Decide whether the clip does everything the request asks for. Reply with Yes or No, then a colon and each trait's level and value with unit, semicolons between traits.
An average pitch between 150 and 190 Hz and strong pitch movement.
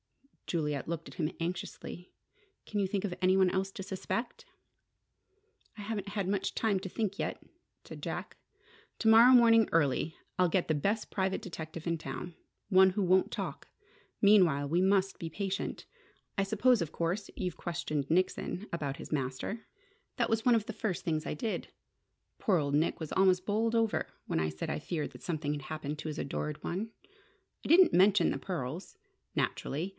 No: medium, 185 Hz; average, 4.4 semitones